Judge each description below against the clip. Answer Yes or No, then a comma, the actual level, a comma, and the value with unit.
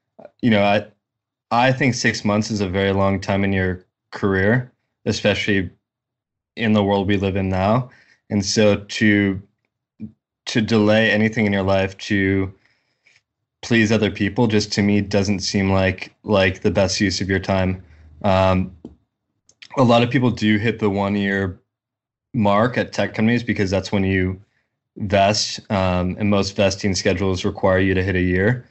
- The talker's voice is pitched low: Yes, low, 100 Hz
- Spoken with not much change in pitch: Yes, narrow, 2.2 semitones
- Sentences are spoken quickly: No, average, 165 wpm